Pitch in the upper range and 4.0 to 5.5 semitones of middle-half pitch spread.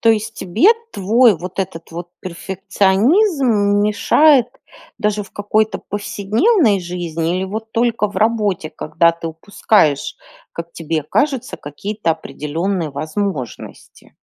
Yes: high, 200 Hz; average, 4.8 semitones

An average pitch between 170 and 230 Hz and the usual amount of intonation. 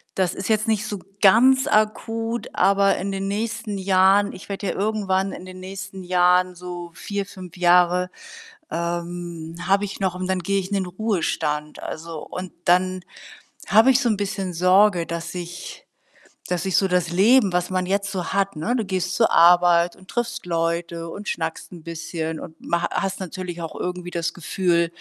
No: medium, 185 Hz; narrow, 2.3 semitones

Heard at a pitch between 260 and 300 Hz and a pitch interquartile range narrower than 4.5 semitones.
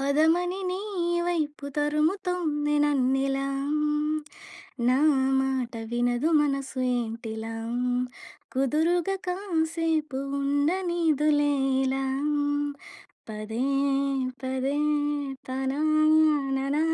Yes: very high, 290 Hz; average, 3.3 semitones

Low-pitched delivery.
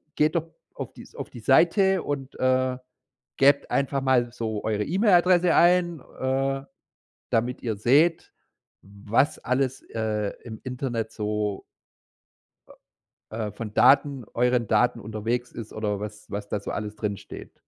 Yes: low, 125 Hz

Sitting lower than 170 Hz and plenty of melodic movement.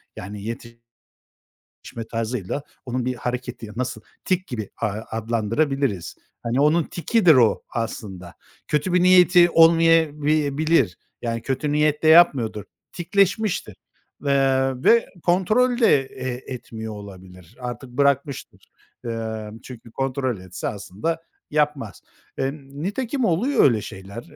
Yes: low, 135 Hz; wide, 6.1 semitones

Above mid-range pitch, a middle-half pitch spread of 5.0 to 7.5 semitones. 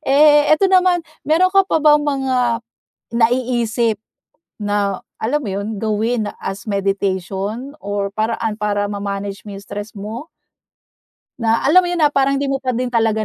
Yes: high, 230 Hz; average, 5.3 semitones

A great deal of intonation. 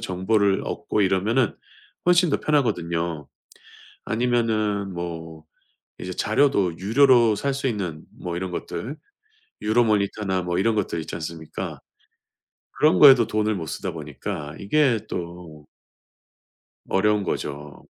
No: average, 4.9 semitones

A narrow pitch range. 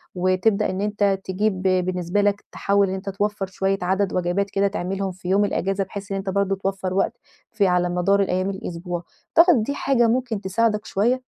Yes: narrow, 1.7 semitones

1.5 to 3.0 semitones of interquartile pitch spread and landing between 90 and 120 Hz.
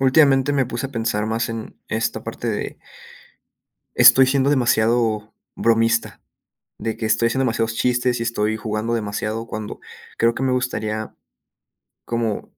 Yes: narrow, 2.5 semitones; low, 115 Hz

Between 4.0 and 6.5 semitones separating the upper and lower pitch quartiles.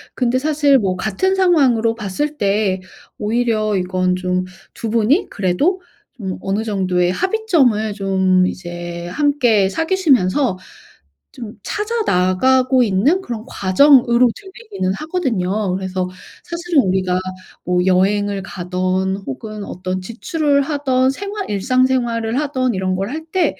No: wide, 7.1 semitones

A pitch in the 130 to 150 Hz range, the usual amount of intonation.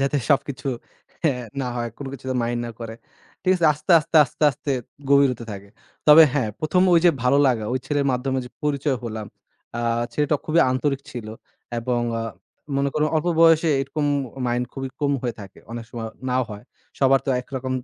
Yes: low, 135 Hz; average, 3.3 semitones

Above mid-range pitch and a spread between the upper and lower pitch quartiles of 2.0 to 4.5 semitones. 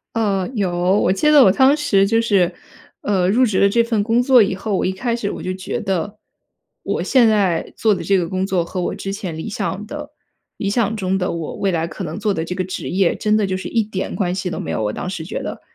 Yes: high, 195 Hz; average, 3.2 semitones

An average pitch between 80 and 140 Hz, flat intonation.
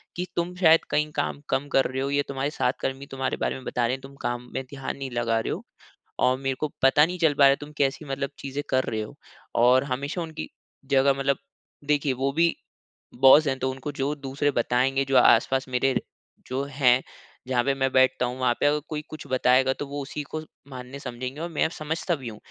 Yes: low, 135 Hz; narrow, 2.0 semitones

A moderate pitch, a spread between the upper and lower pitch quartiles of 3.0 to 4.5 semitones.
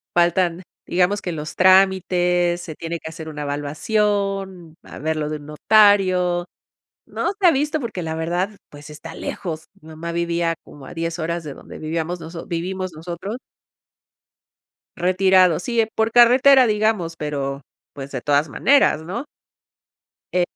Yes: medium, 175 Hz; average, 3.4 semitones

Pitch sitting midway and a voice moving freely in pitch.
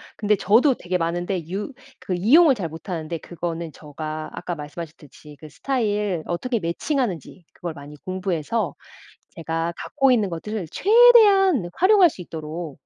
Yes: medium, 180 Hz; wide, 6.3 semitones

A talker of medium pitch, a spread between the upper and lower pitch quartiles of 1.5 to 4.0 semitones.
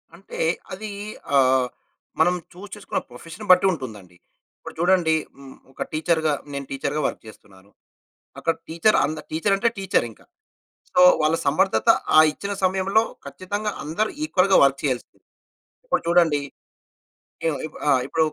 No: medium, 160 Hz; wide, 5.6 semitones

